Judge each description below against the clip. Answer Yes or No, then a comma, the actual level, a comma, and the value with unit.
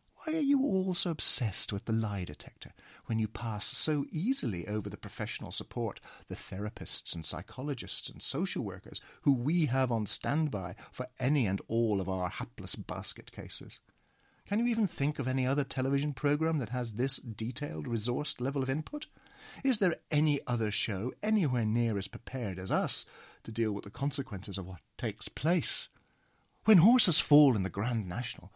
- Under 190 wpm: Yes, average, 175 wpm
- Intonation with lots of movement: Yes, wide, 5.9 semitones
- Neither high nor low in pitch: No, low, 120 Hz